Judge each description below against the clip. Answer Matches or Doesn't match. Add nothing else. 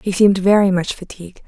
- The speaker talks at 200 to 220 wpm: Matches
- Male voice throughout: Doesn't match